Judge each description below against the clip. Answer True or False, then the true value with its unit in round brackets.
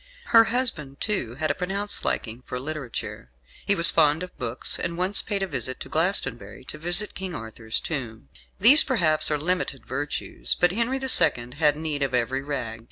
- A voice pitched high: False (155 Hz)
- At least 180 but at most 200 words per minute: True (185 wpm)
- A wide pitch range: True (6.6 semitones)